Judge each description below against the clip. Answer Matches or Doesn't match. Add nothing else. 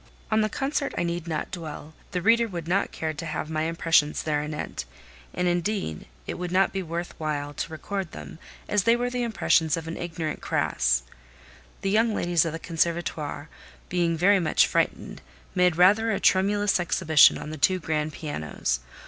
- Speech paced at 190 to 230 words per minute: Doesn't match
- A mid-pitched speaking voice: Matches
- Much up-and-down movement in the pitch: Doesn't match